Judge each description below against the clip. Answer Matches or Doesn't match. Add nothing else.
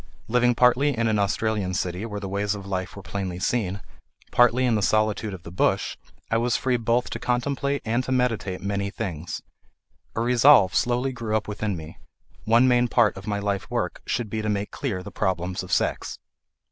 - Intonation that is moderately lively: Matches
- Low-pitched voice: Matches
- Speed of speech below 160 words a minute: Doesn't match